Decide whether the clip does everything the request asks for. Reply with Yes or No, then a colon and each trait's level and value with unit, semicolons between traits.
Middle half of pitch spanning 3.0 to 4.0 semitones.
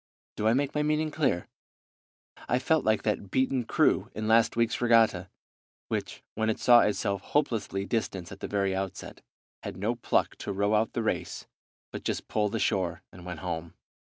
Yes: average, 3.6 semitones